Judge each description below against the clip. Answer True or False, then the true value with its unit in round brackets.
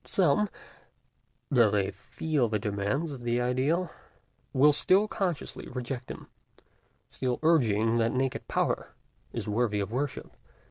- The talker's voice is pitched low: True (125 Hz)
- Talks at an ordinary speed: False (130 wpm)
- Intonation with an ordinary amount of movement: True (4.8 semitones)